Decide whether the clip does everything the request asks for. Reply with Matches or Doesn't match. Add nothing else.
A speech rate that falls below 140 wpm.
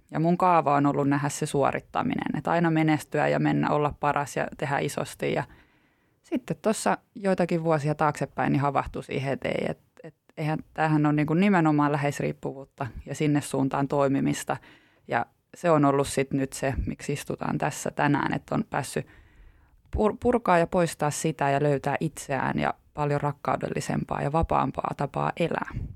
Doesn't match